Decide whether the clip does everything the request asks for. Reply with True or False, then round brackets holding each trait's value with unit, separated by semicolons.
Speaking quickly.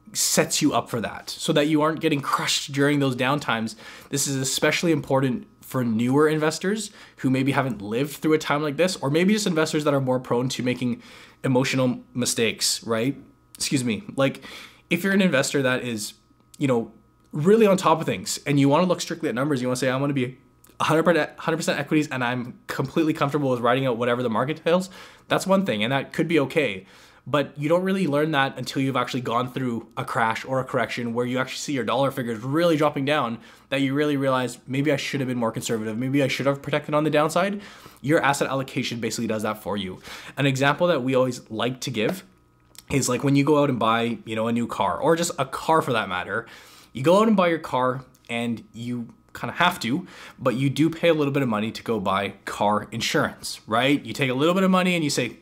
True (235 wpm)